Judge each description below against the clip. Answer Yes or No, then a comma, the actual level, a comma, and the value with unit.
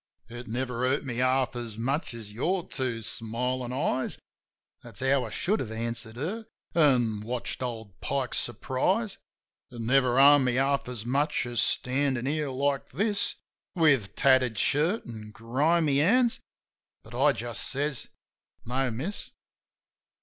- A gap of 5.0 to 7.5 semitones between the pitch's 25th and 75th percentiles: No, average, 3.3 semitones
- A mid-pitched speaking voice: No, low, 130 Hz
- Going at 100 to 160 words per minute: Yes, average, 150 wpm